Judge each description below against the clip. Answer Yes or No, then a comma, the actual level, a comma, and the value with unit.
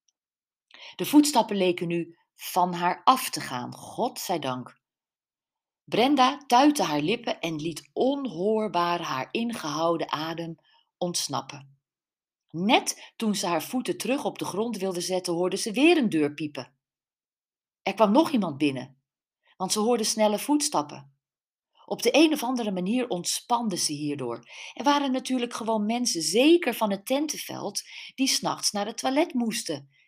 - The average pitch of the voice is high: Yes, high, 195 Hz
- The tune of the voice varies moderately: No, wide, 6.9 semitones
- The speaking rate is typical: Yes, average, 150 wpm